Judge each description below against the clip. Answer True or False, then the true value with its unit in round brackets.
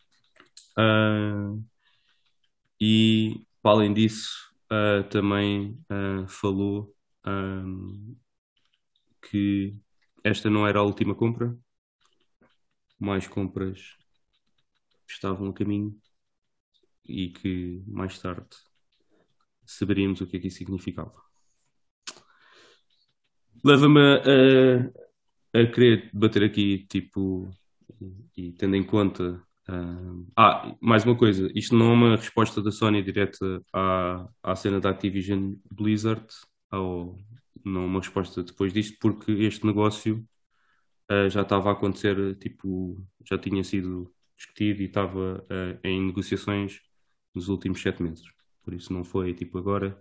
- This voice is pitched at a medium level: False (100 Hz)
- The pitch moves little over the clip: True (2.2 semitones)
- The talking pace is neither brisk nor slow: False (120 wpm)